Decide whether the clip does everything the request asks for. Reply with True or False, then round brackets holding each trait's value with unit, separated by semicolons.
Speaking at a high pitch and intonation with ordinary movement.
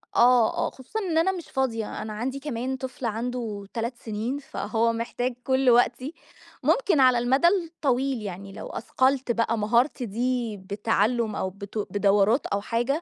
True (240 Hz; 3.3 semitones)